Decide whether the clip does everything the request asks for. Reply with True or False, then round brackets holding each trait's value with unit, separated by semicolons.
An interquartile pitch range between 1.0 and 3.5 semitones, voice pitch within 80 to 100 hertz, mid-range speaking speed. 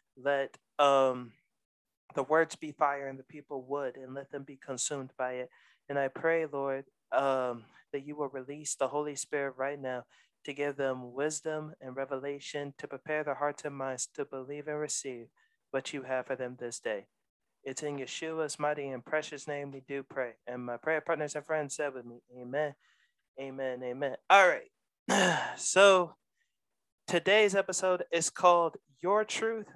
False (2.4 semitones; 140 Hz; 170 wpm)